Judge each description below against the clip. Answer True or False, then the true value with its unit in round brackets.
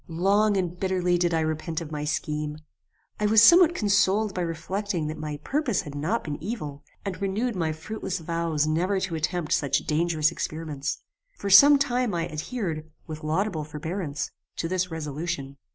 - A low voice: False (170 Hz)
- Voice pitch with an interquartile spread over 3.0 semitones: True (4.3 semitones)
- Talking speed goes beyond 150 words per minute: True (170 wpm)